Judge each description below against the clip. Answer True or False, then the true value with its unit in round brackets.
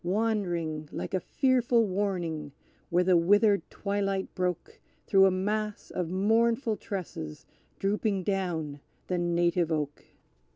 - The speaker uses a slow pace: True (120 wpm)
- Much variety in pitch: False (3.2 semitones)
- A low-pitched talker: False (190 Hz)